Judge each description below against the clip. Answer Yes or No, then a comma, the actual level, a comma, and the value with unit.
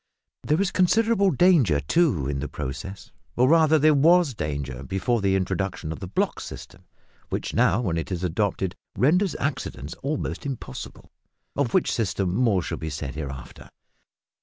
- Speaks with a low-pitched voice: Yes, low, 100 Hz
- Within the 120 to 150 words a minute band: No, average, 160 wpm